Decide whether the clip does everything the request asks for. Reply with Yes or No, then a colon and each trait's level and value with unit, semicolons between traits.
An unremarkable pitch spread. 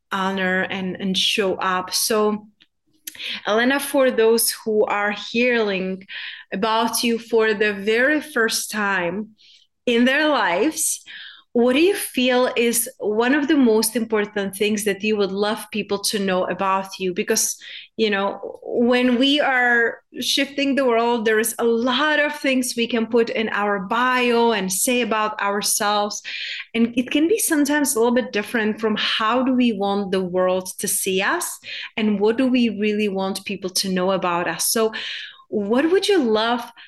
Yes: average, 3.6 semitones